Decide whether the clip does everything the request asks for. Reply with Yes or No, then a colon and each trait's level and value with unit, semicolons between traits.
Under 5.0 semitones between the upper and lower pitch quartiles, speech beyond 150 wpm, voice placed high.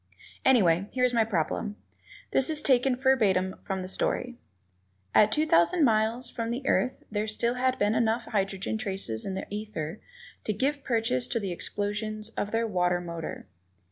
Yes: average, 4.3 semitones; average, 170 wpm; high, 215 Hz